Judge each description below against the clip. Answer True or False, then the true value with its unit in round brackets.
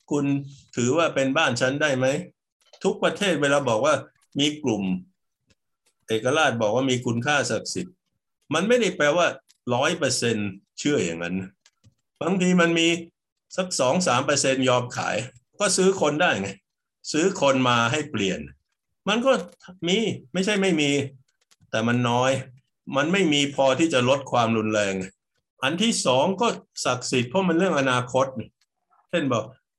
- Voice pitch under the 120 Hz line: False (140 Hz)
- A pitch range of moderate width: False (5.8 semitones)